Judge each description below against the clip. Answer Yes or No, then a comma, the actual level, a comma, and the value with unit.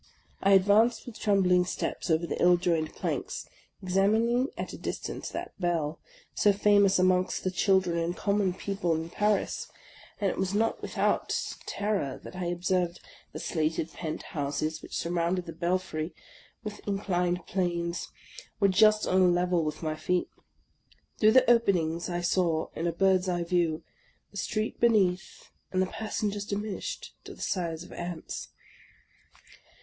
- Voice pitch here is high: No, medium, 180 Hz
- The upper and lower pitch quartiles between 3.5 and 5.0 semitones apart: No, average, 2.9 semitones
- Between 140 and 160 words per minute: Yes, average, 155 wpm